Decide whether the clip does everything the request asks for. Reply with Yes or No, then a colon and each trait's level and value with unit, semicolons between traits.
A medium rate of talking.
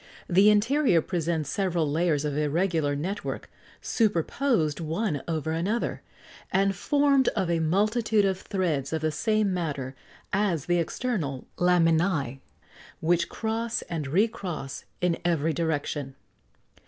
No: slow, 130 wpm